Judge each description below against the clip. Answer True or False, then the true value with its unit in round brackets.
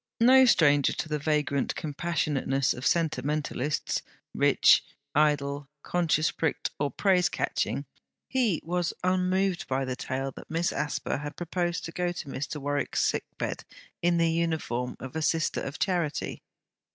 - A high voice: False (155 Hz)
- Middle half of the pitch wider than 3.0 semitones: True (3.4 semitones)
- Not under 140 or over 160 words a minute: True (145 wpm)